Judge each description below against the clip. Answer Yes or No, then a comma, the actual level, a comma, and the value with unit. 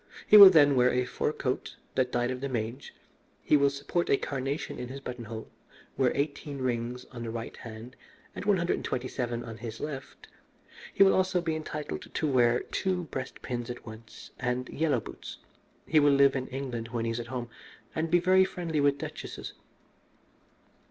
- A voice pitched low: Yes, low, 130 Hz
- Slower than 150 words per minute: No, average, 190 wpm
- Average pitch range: Yes, average, 3.8 semitones